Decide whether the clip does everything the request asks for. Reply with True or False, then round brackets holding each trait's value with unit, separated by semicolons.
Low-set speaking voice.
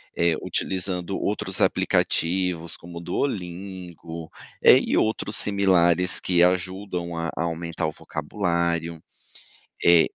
True (85 Hz)